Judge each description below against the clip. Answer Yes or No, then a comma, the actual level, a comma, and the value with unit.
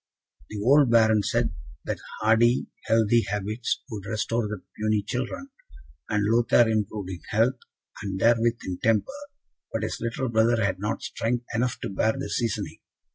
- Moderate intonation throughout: No, narrow, 1.9 semitones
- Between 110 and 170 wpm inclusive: Yes, average, 155 wpm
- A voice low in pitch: Yes, low, 110 Hz